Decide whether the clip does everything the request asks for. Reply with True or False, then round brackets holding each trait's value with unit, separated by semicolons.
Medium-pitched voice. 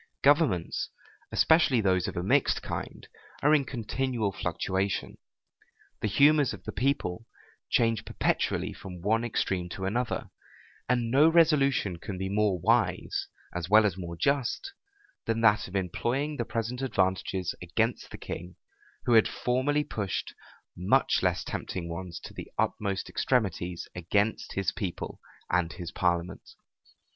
False (105 Hz)